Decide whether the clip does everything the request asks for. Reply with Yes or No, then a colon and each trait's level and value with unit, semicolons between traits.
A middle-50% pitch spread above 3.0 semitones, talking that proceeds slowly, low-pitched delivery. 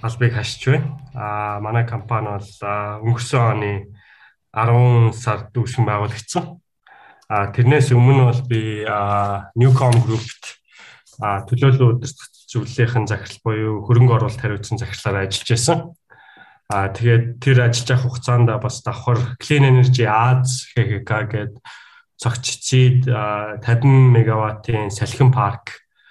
No: average, 2.7 semitones; slow, 120 wpm; low, 120 Hz